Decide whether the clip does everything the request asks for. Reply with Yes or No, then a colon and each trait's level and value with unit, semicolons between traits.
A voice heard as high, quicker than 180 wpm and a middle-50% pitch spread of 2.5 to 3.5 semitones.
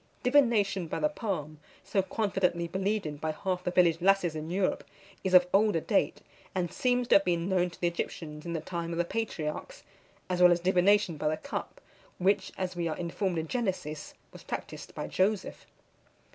No: medium, 180 Hz; average, 190 wpm; average, 2.8 semitones